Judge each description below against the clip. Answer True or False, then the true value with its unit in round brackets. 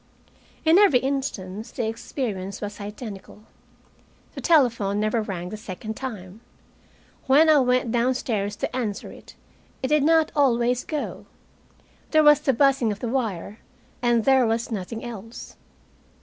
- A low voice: False (235 Hz)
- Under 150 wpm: True (140 wpm)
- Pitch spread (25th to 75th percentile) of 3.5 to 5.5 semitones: True (4.2 semitones)